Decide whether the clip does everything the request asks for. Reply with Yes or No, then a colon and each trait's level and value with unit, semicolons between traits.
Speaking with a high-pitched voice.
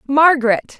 Yes: very high, 270 Hz